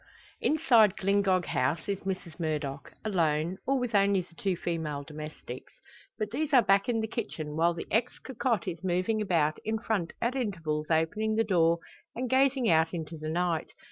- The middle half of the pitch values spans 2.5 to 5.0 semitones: No, wide, 5.4 semitones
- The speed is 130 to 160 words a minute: No, average, 175 wpm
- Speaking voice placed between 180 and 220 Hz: Yes, medium, 185 Hz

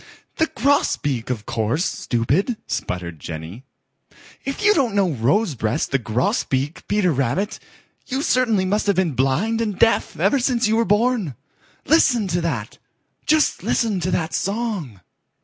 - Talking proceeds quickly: No, average, 145 wpm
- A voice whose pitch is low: No, medium, 185 Hz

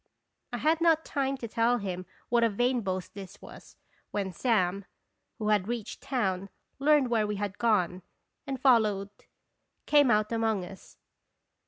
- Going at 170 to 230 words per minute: No, average, 160 wpm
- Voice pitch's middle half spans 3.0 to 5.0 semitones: Yes, average, 4.0 semitones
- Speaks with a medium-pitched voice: No, high, 220 Hz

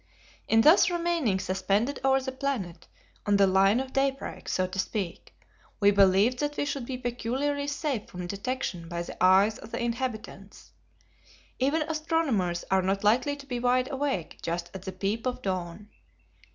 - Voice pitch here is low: No, high, 230 Hz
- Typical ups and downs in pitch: No, wide, 6.0 semitones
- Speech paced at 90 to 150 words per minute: No, average, 165 wpm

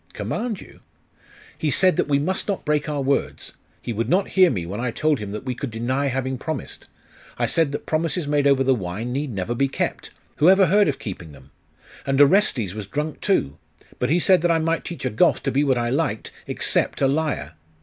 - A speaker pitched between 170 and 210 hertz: No, medium, 140 Hz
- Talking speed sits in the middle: No, fast, 220 wpm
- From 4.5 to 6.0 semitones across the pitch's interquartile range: Yes, average, 5.2 semitones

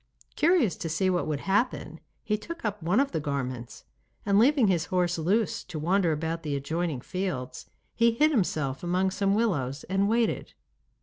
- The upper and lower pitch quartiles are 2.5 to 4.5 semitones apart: No, wide, 5.4 semitones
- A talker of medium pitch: Yes, medium, 180 Hz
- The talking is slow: No, average, 175 wpm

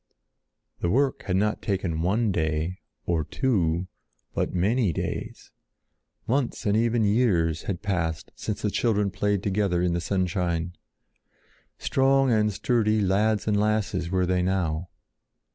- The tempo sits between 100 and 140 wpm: Yes, slow, 135 wpm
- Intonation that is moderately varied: Yes, average, 3.6 semitones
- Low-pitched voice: Yes, low, 100 Hz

